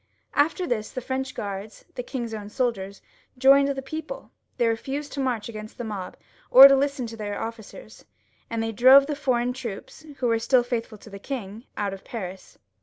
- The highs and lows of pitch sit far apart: No, average, 3.9 semitones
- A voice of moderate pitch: No, high, 240 Hz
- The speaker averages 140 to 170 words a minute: No, average, 190 wpm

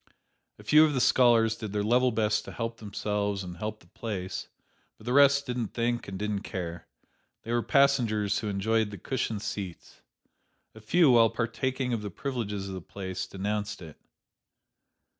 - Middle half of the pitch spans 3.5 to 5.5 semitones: No, average, 3.1 semitones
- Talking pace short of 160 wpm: No, average, 175 wpm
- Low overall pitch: Yes, low, 110 Hz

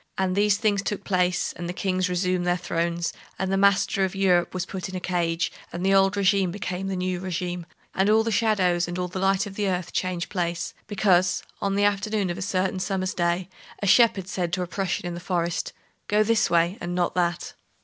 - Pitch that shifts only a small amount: Yes, narrow, 1.8 semitones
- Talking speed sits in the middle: No, fast, 220 wpm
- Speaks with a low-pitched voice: No, medium, 185 Hz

